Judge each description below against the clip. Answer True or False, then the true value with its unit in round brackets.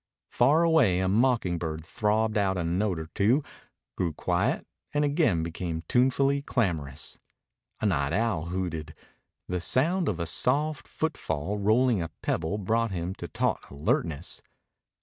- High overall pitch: False (100 Hz)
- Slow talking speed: False (145 wpm)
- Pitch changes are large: True (6.8 semitones)